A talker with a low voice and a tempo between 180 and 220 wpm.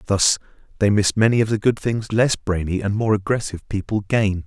Yes: low, 105 Hz; average, 200 wpm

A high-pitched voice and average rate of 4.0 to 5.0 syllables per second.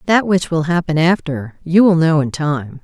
No: medium, 160 Hz; 4.6 syllables/s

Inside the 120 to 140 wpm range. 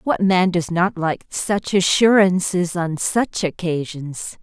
Yes: slow, 135 wpm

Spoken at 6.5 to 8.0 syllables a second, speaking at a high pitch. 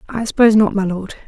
Yes: 7.0 syllables/s; high, 210 Hz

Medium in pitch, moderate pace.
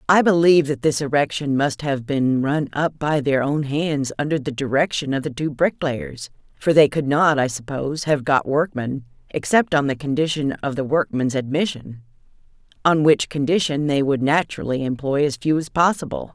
Yes: medium, 145 Hz; average, 180 wpm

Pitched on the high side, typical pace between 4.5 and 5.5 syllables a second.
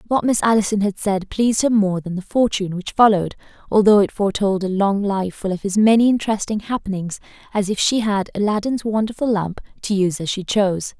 No: high, 205 Hz; 6.0 syllables/s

